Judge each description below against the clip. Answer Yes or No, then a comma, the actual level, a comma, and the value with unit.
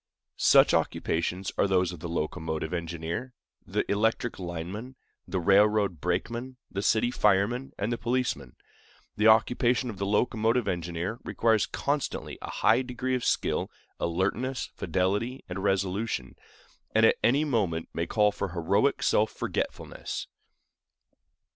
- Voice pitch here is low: Yes, low, 100 Hz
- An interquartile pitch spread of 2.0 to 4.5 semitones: No, average, 5.0 semitones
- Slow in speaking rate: Yes, slow, 130 wpm